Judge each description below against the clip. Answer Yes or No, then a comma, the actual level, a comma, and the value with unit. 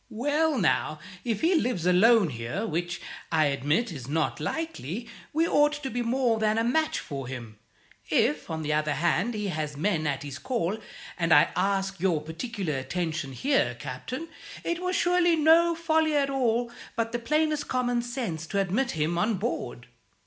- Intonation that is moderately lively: No, wide, 9.0 semitones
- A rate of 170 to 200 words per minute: Yes, average, 175 wpm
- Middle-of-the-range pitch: No, high, 210 Hz